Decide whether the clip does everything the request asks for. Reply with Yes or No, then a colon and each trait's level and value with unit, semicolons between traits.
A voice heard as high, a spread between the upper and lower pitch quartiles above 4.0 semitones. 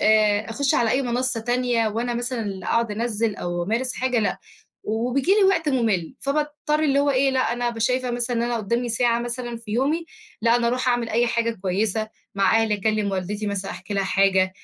No: high, 235 Hz; average, 2.9 semitones